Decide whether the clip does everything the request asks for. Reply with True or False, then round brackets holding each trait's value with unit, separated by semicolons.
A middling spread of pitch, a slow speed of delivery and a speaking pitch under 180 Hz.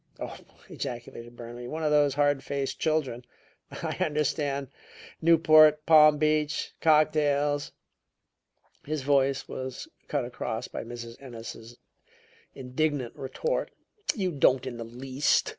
True (3.4 semitones; 120 wpm; 140 Hz)